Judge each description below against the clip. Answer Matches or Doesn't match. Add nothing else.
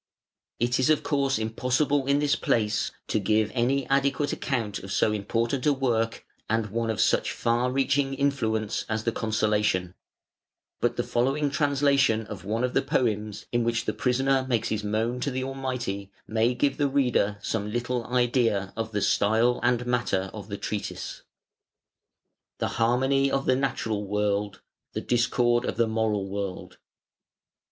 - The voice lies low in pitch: Matches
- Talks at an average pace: Matches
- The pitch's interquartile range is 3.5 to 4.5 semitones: Matches